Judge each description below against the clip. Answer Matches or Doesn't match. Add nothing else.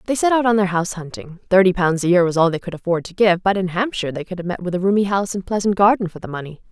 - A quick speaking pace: Matches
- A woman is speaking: Matches